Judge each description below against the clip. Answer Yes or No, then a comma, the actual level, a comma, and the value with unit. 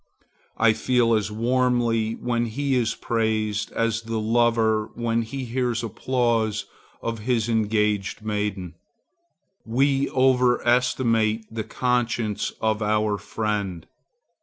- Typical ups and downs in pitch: No, narrow, 2.0 semitones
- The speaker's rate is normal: No, slow, 110 wpm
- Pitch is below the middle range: Yes, low, 115 Hz